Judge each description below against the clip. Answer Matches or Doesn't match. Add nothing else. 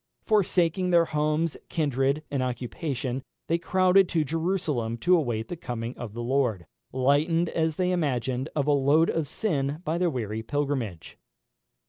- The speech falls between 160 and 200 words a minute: Doesn't match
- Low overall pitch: Doesn't match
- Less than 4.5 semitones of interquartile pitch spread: Doesn't match